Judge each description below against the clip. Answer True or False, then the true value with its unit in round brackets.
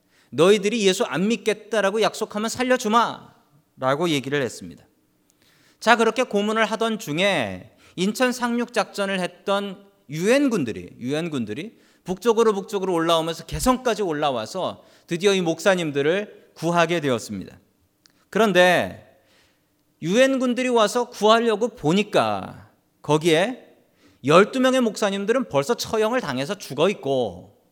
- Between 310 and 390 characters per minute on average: False (295 characters per minute)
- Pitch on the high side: True (200 Hz)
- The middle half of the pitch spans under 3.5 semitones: False (5.5 semitones)